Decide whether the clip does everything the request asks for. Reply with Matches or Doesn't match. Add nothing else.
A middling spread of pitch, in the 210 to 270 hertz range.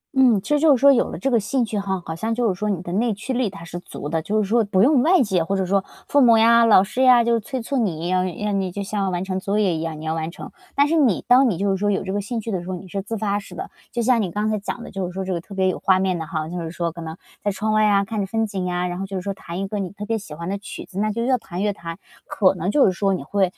Doesn't match